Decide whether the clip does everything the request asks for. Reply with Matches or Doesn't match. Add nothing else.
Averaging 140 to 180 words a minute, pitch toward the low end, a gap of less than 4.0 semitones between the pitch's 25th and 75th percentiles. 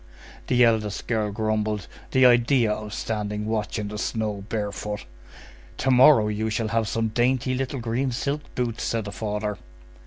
Matches